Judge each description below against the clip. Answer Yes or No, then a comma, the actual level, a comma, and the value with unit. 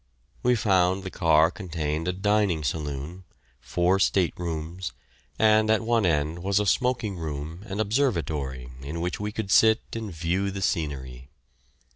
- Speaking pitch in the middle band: No, very low, 90 Hz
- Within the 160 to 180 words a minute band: No, average, 150 wpm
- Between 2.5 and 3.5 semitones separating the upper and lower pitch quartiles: No, average, 4.9 semitones